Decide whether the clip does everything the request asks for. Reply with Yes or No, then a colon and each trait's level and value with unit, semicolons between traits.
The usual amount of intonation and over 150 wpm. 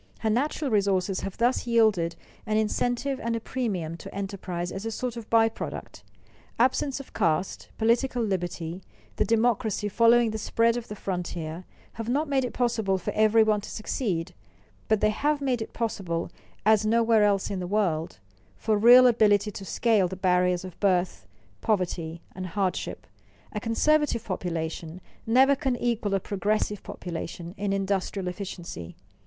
Yes: average, 4.1 semitones; average, 160 wpm